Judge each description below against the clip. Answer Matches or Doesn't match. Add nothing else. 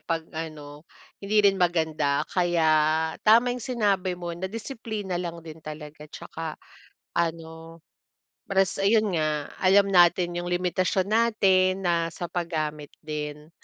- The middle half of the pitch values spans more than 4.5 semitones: Doesn't match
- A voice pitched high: Doesn't match